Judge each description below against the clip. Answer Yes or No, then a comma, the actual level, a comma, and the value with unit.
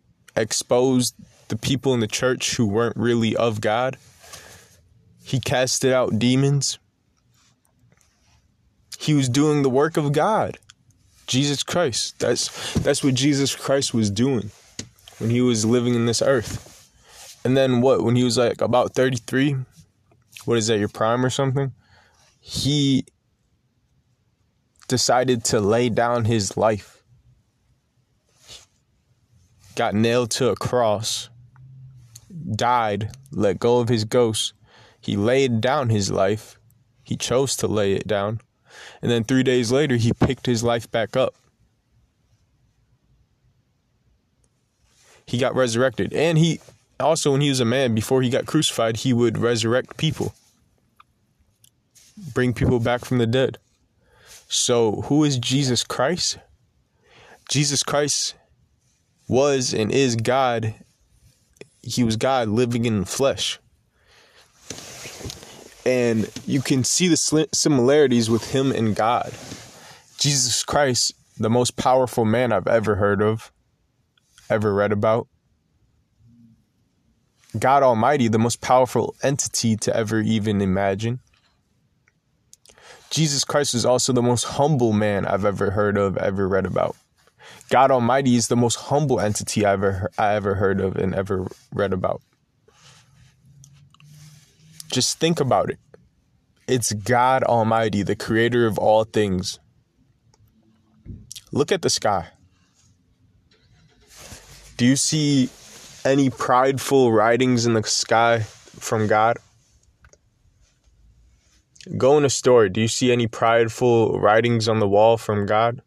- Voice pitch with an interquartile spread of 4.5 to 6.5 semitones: No, average, 3.0 semitones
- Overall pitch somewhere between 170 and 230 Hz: No, low, 120 Hz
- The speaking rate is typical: No, slow, 125 wpm